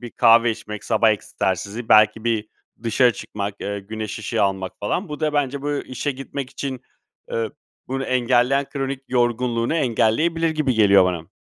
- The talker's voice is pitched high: No, low, 120 Hz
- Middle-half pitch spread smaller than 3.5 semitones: No, average, 4.1 semitones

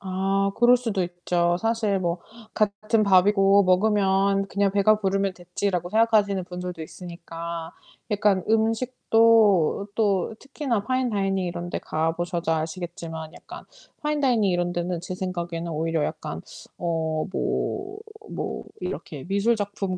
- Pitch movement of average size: Yes, average, 3.5 semitones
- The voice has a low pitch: No, high, 195 Hz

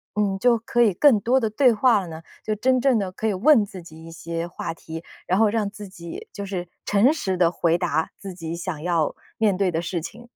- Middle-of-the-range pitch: No, high, 195 Hz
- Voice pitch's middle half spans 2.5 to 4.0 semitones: No, average, 4.7 semitones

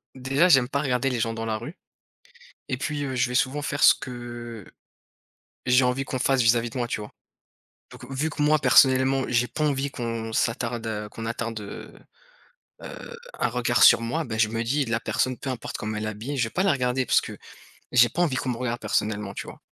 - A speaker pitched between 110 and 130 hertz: Yes, low, 125 Hz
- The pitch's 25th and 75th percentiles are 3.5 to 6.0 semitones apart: No, average, 2.9 semitones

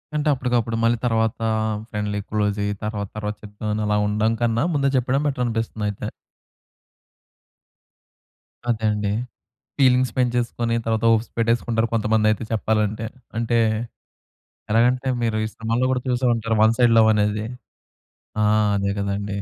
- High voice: No, low, 115 Hz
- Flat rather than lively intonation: Yes, narrow, 2.1 semitones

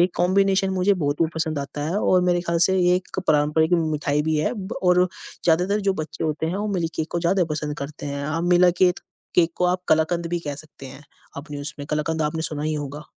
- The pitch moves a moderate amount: Yes, average, 3.0 semitones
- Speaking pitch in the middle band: Yes, medium, 160 Hz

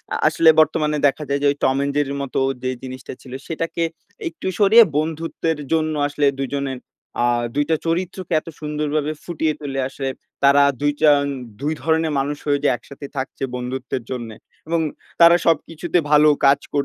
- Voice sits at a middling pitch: Yes, medium, 150 Hz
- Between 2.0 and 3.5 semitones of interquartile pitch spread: Yes, narrow, 2.6 semitones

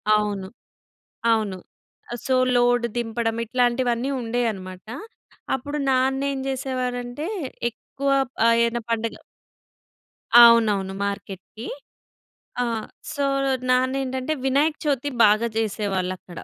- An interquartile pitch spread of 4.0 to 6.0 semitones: No, average, 3.4 semitones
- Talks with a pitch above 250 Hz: No, high, 240 Hz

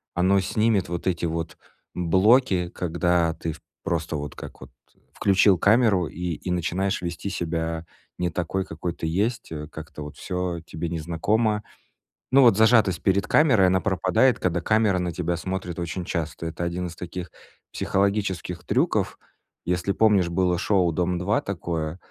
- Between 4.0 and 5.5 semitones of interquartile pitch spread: No, average, 2.7 semitones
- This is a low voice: Yes, very low, 90 Hz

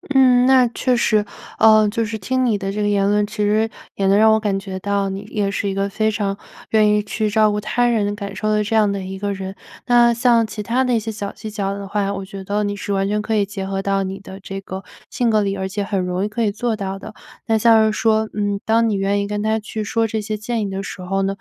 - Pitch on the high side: Yes, high, 210 Hz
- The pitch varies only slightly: Yes, narrow, 1.9 semitones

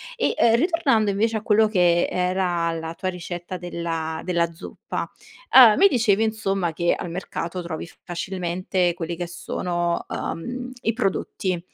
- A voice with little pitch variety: No, average, 4.0 semitones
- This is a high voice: No, medium, 180 Hz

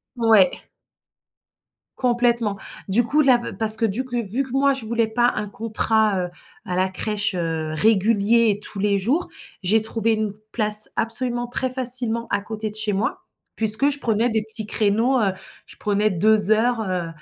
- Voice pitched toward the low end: No, high, 220 Hz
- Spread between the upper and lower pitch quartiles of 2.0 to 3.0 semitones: Yes, narrow, 2.5 semitones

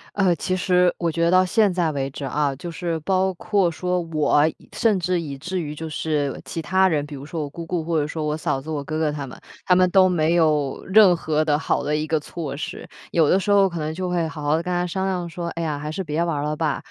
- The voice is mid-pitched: Yes, medium, 165 Hz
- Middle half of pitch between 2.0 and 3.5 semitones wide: Yes, average, 3.2 semitones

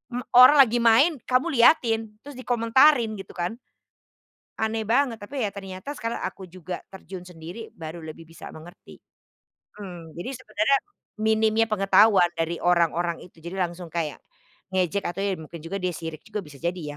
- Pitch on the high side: Yes, high, 195 Hz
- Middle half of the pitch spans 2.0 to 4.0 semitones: No, average, 4.8 semitones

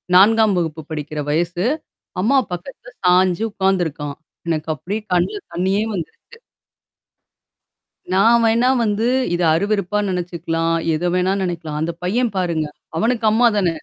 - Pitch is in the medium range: Yes, medium, 180 Hz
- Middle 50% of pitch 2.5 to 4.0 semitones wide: No, average, 4.5 semitones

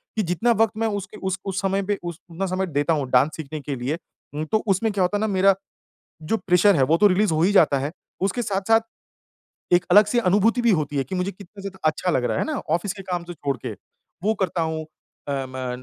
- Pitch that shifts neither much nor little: Yes, average, 4.5 semitones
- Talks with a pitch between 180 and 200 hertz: Yes, medium, 185 Hz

